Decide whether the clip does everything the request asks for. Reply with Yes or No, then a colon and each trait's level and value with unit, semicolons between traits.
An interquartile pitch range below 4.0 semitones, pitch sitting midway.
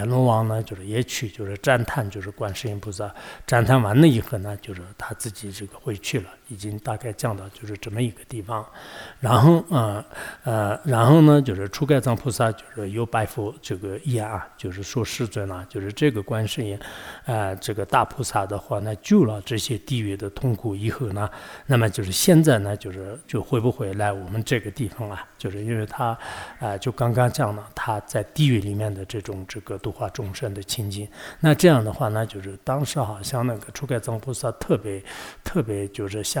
No: average, 3.6 semitones; low, 110 Hz